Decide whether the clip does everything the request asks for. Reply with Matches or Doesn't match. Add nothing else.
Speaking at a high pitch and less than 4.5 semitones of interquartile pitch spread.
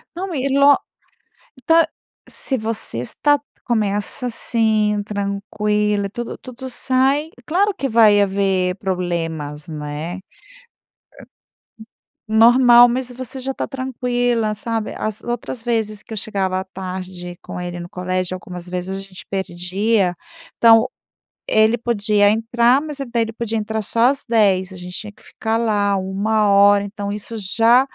Matches